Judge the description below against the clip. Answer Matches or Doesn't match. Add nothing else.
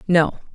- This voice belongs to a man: Doesn't match